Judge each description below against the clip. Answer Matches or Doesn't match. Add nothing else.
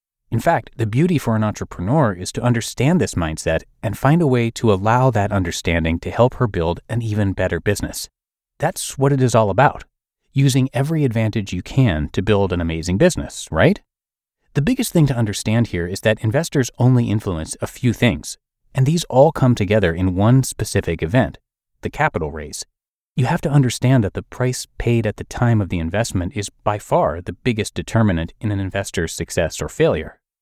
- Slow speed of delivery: Doesn't match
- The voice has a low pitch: Matches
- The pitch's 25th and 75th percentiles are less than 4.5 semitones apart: Doesn't match